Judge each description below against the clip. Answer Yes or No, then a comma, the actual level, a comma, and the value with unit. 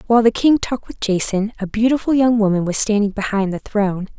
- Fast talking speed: Yes, fast, 215 wpm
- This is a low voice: No, high, 215 Hz